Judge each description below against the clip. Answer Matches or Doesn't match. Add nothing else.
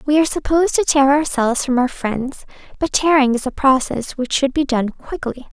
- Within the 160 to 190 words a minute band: Doesn't match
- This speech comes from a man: Doesn't match